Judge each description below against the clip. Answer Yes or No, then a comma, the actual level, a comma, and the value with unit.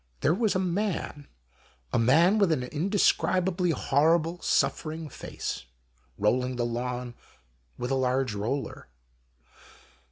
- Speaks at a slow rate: Yes, slow, 120 wpm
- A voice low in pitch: No, medium, 150 Hz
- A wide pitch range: Yes, wide, 5.9 semitones